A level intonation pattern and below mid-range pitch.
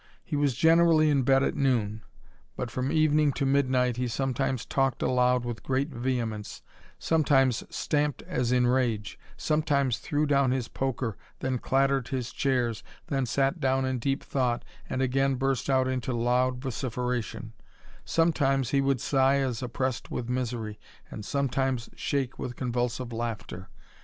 Yes: narrow, 2.0 semitones; low, 130 Hz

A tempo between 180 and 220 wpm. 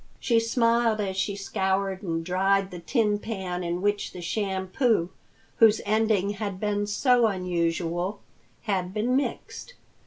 No: slow, 135 wpm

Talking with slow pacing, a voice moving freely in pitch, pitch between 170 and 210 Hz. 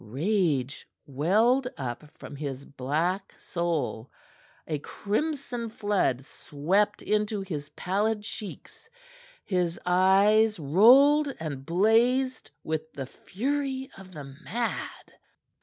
Yes: slow, 100 wpm; wide, 6.9 semitones; high, 190 Hz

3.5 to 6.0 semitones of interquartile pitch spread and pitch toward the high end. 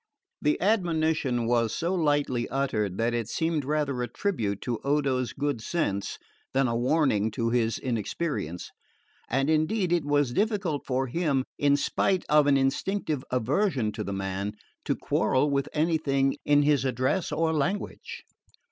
No: average, 4.7 semitones; medium, 140 Hz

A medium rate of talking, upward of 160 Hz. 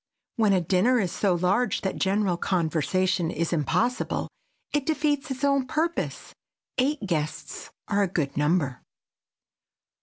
No: slow, 130 wpm; high, 190 Hz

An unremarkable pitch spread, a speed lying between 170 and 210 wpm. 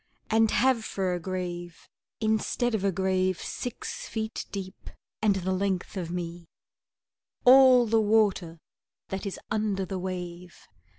No: average, 3.2 semitones; slow, 135 wpm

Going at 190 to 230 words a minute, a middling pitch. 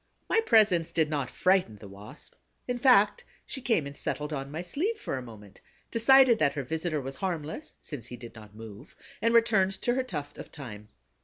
Yes: average, 200 wpm; medium, 155 Hz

